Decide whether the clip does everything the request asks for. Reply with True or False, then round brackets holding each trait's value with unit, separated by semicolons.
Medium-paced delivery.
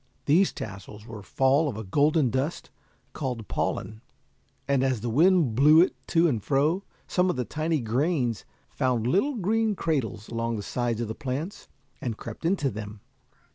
True (170 wpm)